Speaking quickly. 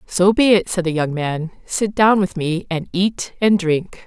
Yes: fast, 220 wpm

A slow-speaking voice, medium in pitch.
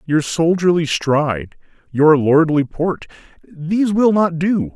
Yes: slow, 115 wpm; medium, 165 Hz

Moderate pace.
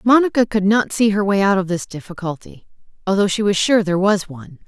No: fast, 220 wpm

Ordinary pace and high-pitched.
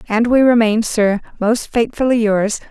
Yes: average, 155 wpm; high, 225 Hz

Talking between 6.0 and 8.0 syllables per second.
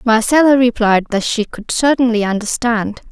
No: 4.9 syllables/s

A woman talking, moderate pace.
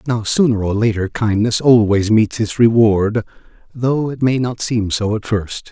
No: male; average, 180 wpm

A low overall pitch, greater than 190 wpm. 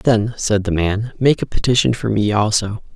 Yes: low, 110 Hz; fast, 205 wpm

